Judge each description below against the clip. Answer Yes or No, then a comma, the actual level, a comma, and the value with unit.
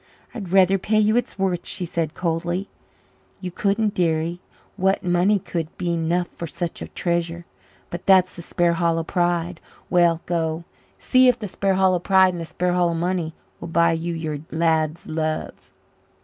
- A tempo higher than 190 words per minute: No, average, 160 wpm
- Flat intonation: Yes, narrow, 2.1 semitones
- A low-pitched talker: No, medium, 175 Hz